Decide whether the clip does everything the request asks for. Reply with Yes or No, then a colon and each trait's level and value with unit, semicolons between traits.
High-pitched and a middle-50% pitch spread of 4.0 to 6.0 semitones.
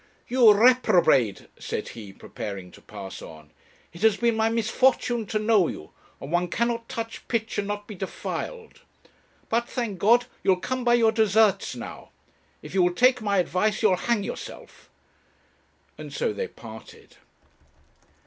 Yes: high, 215 Hz; average, 4.5 semitones